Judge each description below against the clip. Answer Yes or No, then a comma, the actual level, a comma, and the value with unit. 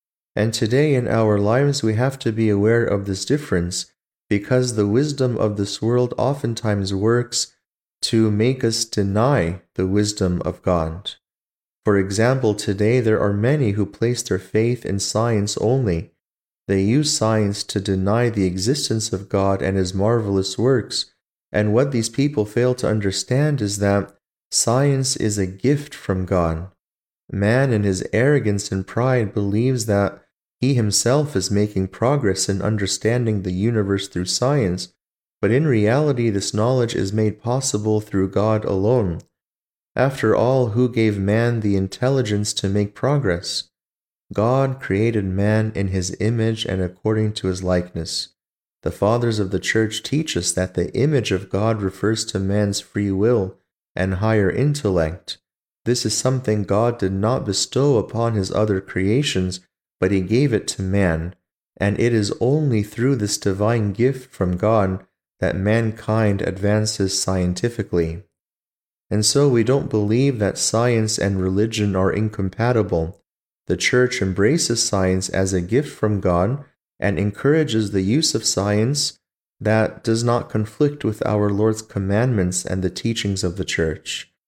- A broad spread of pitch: No, average, 3.6 semitones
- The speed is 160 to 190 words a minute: No, average, 150 wpm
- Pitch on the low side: Yes, low, 105 Hz